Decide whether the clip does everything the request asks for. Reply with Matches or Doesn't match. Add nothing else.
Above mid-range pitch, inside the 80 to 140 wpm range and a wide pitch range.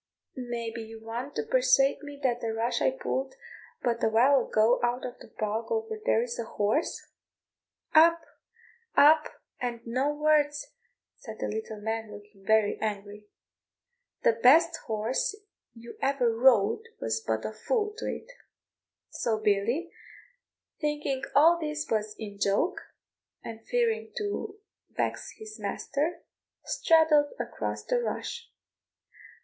Matches